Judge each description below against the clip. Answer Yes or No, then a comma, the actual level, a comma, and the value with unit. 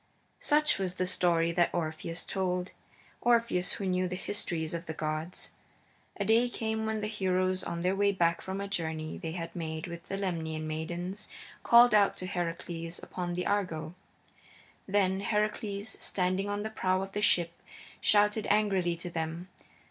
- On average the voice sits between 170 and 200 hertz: Yes, medium, 185 Hz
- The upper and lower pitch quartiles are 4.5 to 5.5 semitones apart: No, average, 3.2 semitones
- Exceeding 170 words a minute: No, average, 165 wpm